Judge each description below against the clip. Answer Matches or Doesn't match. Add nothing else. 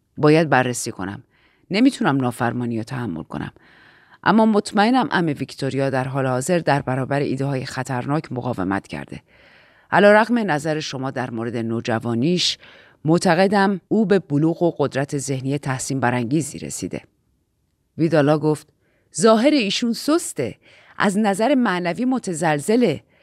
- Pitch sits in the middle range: Matches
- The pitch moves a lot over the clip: Matches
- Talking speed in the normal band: Matches